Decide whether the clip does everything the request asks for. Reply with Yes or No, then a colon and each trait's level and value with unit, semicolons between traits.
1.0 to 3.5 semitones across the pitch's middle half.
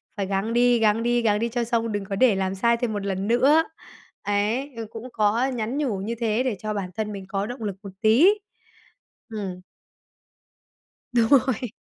Yes: average, 2.9 semitones